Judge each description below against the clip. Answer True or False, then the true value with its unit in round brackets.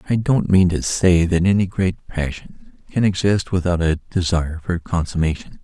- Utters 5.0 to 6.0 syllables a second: False (4.8 syllables/s)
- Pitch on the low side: True (90 Hz)